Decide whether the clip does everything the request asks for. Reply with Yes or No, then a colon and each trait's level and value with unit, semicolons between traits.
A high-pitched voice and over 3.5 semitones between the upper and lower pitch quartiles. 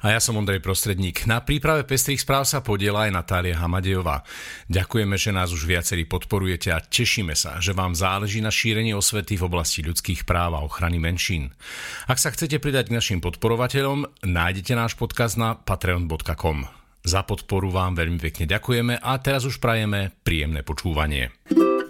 No: very low, 95 Hz; average, 4.9 semitones